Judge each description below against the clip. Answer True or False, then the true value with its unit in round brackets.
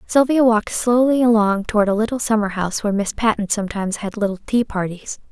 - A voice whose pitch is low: False (215 Hz)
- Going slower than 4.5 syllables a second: False (6.3 syllables/s)